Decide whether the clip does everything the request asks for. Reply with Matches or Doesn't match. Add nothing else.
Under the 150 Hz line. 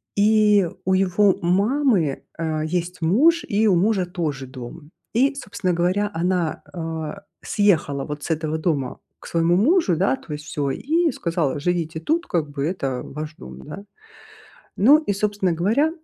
Doesn't match